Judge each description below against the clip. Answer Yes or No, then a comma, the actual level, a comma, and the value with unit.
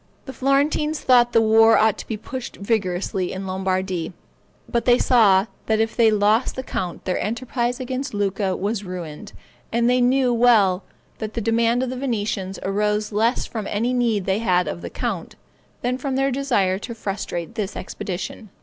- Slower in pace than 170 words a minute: No, average, 175 wpm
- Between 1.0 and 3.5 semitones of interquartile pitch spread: No, average, 4.1 semitones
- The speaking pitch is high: Yes, high, 220 Hz